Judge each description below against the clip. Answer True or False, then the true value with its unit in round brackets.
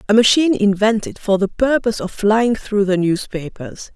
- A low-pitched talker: False (205 Hz)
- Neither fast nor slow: True (165 wpm)